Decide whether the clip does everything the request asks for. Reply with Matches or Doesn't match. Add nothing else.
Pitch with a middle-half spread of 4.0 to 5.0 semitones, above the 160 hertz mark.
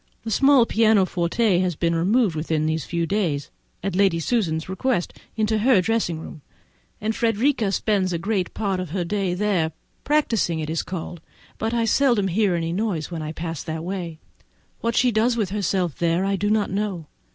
Matches